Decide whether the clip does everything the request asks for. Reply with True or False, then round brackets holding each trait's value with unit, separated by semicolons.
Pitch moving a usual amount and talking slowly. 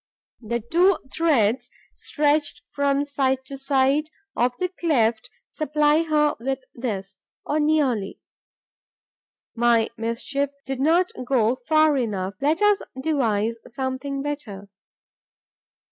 True (4.2 semitones; 110 wpm)